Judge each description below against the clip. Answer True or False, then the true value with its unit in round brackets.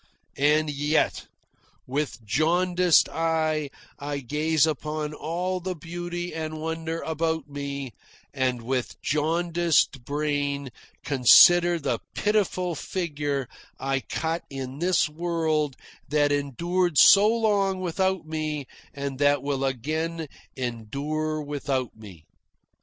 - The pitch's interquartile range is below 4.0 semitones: True (3.2 semitones)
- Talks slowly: True (110 wpm)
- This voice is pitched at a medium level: True (155 Hz)